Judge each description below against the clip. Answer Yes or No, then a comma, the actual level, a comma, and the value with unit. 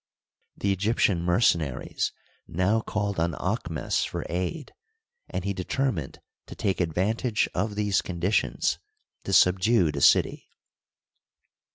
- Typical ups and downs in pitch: Yes, average, 3.4 semitones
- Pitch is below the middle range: Yes, very low, 95 Hz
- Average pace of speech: No, slow, 110 wpm